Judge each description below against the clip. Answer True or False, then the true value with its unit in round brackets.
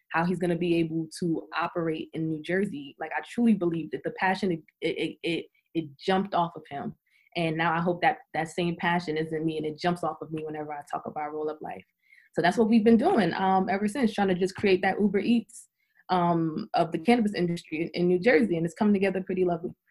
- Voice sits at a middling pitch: True (175 Hz)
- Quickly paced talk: True (240 wpm)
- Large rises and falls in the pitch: False (2.9 semitones)